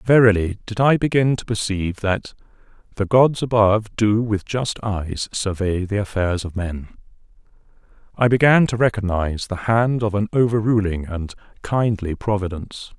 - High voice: No, low, 105 Hz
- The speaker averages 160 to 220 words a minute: No, average, 145 wpm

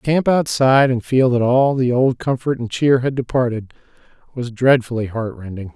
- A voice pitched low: Yes, low, 125 Hz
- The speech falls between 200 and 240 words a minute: No, average, 175 wpm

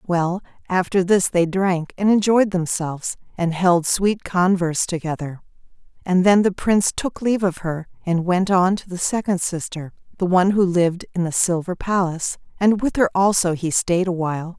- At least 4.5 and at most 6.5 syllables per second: Yes, 5.0 syllables/s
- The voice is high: No, medium, 180 Hz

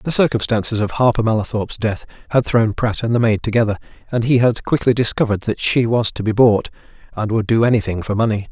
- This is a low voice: Yes, low, 115 Hz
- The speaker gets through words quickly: Yes, fast, 210 wpm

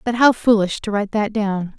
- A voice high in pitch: Yes, high, 210 Hz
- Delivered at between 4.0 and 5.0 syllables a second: No, 5.4 syllables/s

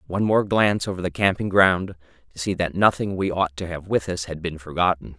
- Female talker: No, male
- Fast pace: Yes, fast, 230 wpm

